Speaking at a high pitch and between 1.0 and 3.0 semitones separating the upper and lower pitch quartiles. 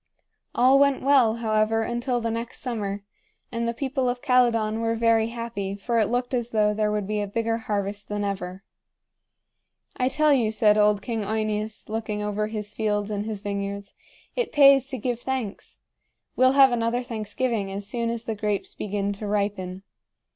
Yes: high, 220 Hz; average, 2.7 semitones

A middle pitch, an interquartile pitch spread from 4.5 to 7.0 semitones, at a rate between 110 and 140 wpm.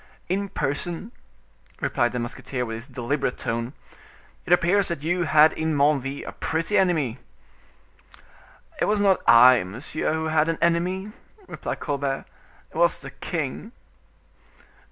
Yes: medium, 155 Hz; average, 5.1 semitones; slow, 135 wpm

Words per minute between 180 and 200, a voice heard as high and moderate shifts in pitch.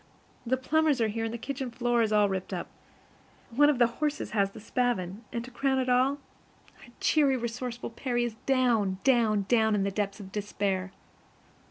Yes: average, 185 wpm; high, 235 Hz; average, 3.7 semitones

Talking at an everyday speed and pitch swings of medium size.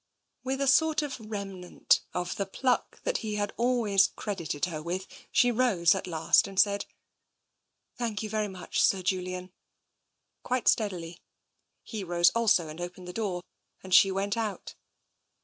Yes: average, 160 wpm; average, 3.8 semitones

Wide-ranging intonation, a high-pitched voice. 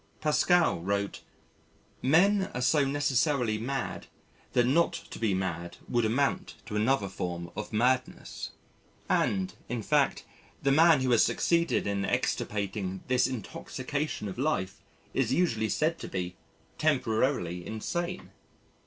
No: wide, 6.4 semitones; low, 125 Hz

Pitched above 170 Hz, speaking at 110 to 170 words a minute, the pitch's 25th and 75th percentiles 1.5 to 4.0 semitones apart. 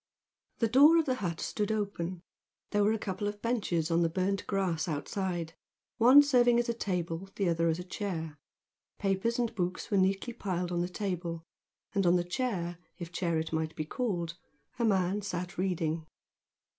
No: medium, 185 Hz; average, 180 wpm; average, 3.6 semitones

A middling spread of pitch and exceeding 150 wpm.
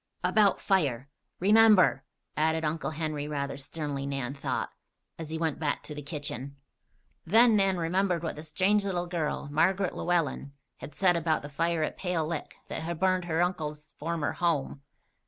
Yes: average, 3.3 semitones; average, 165 wpm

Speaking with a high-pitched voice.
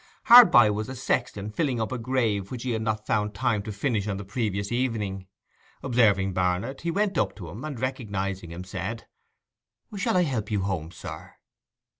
No: low, 110 Hz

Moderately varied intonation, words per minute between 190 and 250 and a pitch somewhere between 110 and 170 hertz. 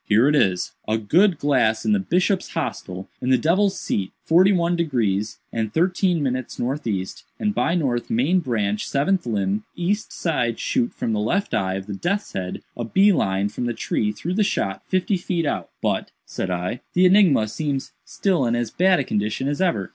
No: wide, 9.0 semitones; average, 195 wpm; low, 135 Hz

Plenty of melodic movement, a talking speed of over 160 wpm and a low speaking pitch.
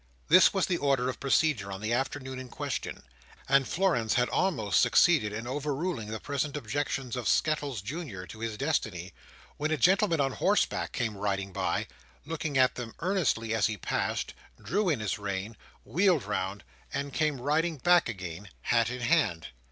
Yes: wide, 6.2 semitones; average, 170 wpm; low, 130 Hz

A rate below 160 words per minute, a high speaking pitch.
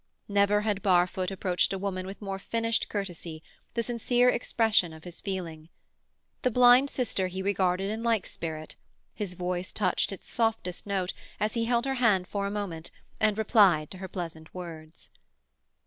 No: average, 165 wpm; high, 195 Hz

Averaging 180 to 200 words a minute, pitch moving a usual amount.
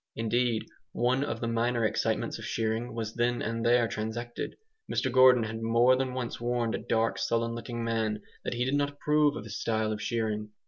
No: average, 195 wpm; narrow, 1.6 semitones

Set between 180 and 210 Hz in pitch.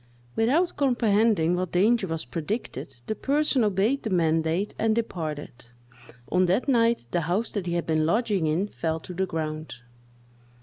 Yes: medium, 185 Hz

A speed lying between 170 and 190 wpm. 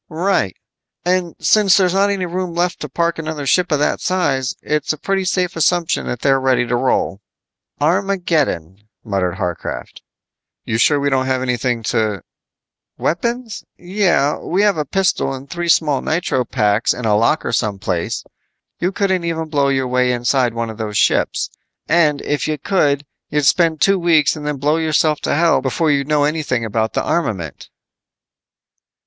Yes: average, 175 wpm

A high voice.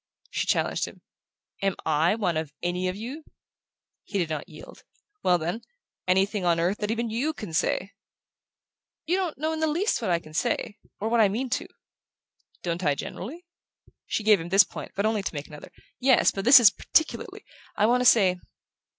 Yes: high, 200 Hz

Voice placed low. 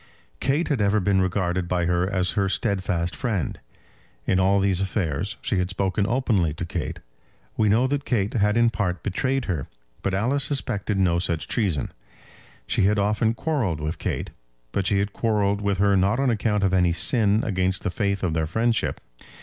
Yes: low, 100 Hz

